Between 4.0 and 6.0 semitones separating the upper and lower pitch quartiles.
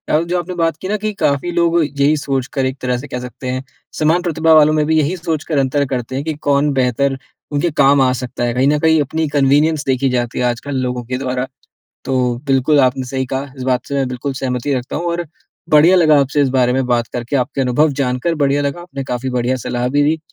No: average, 3.3 semitones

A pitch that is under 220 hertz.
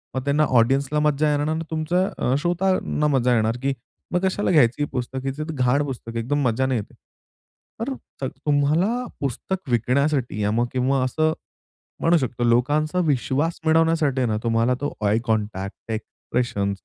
Yes: low, 135 Hz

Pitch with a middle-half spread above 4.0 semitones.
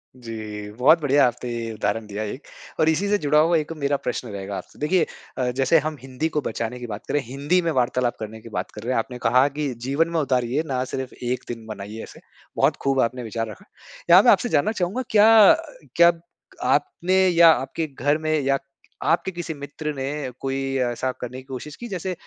Yes: average, 4.7 semitones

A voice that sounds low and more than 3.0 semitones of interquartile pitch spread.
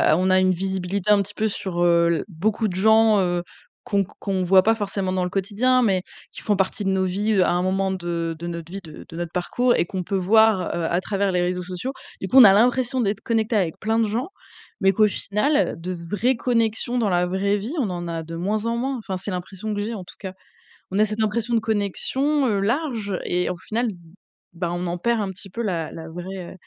No: high, 195 Hz; average, 3.5 semitones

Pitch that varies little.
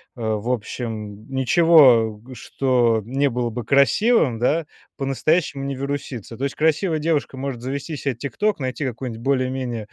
No: average, 3.3 semitones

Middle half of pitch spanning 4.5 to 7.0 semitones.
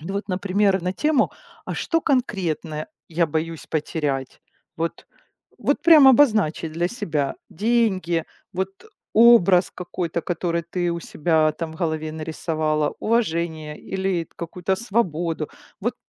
No: average, 3.8 semitones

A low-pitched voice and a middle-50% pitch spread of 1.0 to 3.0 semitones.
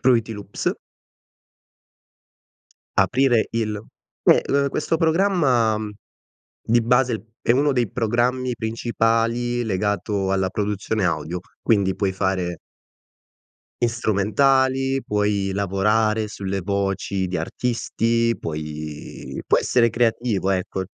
No: low, 110 Hz; average, 3.8 semitones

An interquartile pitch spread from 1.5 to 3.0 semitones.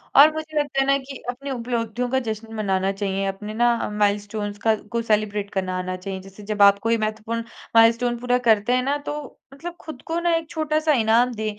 No: average, 4.6 semitones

